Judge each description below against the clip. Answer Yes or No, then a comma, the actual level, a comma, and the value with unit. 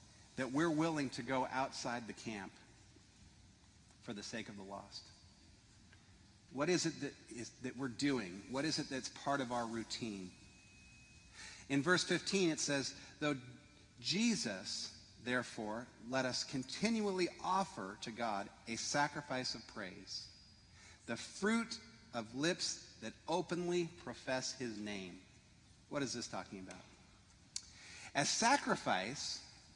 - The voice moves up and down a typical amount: No, wide, 5.8 semitones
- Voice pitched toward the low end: Yes, low, 115 Hz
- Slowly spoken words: Yes, slow, 130 wpm